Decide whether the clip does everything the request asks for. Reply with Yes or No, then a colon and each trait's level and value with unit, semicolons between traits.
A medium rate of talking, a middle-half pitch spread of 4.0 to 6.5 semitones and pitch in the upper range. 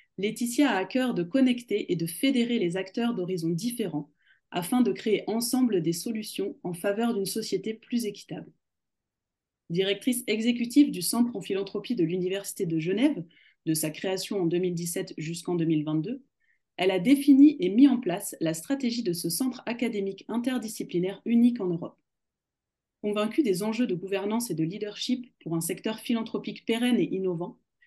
Yes: average, 160 wpm; average, 5.1 semitones; high, 210 Hz